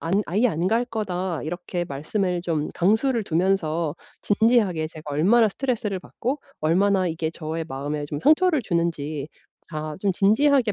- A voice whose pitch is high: No, medium, 180 Hz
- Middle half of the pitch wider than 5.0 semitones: Yes, wide, 5.5 semitones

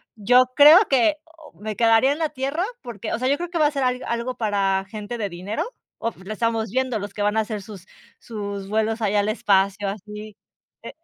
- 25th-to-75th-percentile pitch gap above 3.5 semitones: Yes, average, 3.9 semitones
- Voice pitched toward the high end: Yes, high, 220 Hz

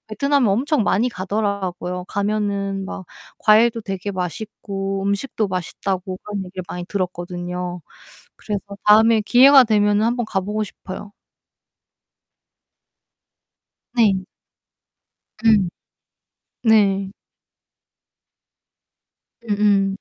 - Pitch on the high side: Yes, high, 200 Hz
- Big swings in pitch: No, narrow, 2.4 semitones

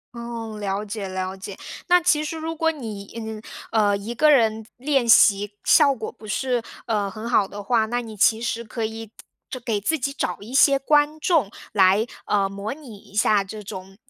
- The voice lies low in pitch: No, high, 220 Hz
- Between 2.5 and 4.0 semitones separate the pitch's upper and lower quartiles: No, average, 4.6 semitones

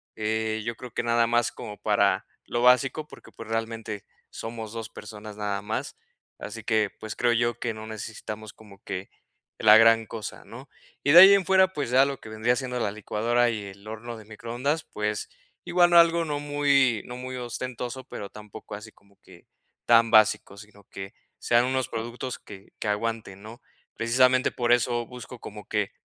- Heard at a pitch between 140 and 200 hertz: No, low, 115 Hz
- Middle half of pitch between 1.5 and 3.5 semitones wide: Yes, average, 2.8 semitones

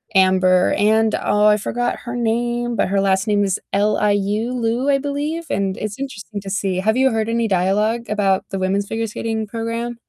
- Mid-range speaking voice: No, high, 215 Hz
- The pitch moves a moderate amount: Yes, average, 3.0 semitones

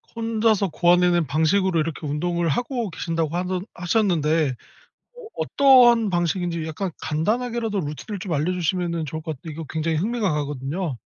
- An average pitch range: Yes, average, 4.4 semitones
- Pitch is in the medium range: Yes, medium, 175 Hz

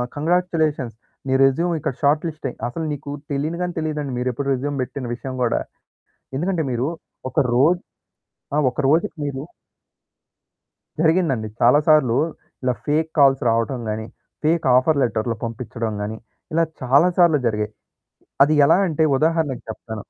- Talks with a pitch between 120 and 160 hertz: Yes, medium, 140 Hz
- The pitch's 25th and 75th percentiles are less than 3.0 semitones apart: No, average, 4.3 semitones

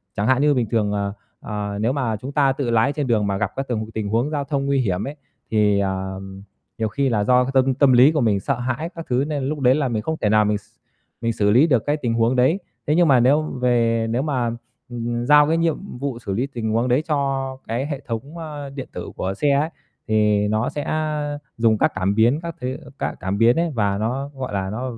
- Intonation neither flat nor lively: Yes, average, 4.4 semitones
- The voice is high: No, low, 125 Hz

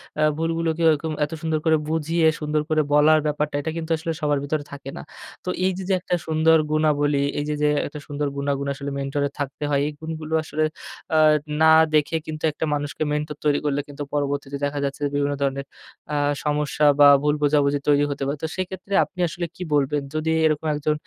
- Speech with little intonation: Yes, narrow, 1.8 semitones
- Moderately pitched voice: Yes, medium, 150 Hz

